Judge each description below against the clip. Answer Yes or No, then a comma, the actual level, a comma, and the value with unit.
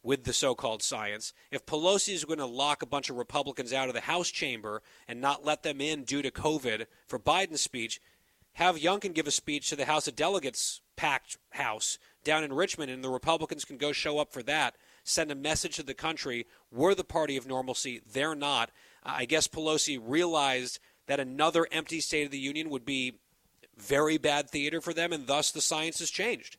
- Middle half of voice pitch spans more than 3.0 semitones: No, narrow, 2.6 semitones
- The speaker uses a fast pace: Yes, fast, 210 wpm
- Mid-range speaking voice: Yes, medium, 150 Hz